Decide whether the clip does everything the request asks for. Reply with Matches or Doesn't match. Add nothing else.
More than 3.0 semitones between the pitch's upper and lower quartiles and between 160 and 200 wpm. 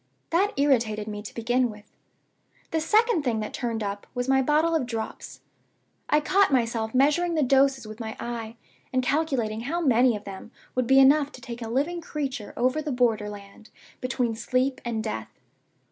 Matches